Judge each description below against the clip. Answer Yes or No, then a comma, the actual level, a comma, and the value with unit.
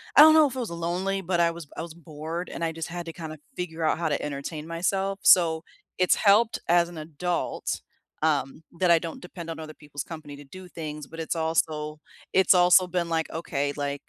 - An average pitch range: No, narrow, 2.3 semitones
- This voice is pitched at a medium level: Yes, medium, 165 Hz